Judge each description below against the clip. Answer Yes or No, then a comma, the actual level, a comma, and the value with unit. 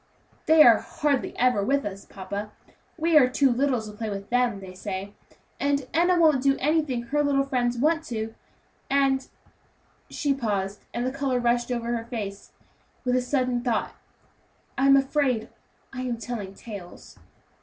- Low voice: No, very high, 250 Hz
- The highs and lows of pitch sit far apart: No, average, 4.0 semitones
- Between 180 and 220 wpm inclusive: No, average, 165 wpm